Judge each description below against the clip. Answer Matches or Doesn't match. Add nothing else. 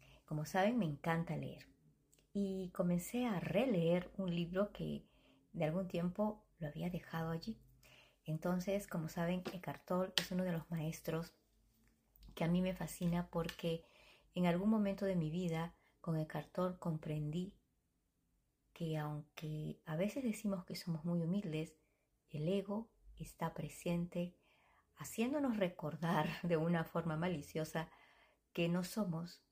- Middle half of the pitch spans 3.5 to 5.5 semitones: Doesn't match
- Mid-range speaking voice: Matches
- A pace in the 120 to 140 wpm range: Matches